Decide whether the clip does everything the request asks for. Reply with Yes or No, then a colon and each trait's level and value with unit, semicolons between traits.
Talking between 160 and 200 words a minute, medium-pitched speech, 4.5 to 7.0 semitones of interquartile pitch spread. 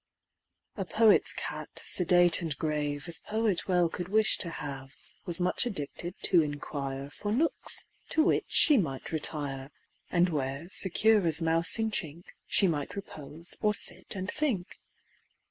No: average, 150 wpm; medium, 170 Hz; average, 5.2 semitones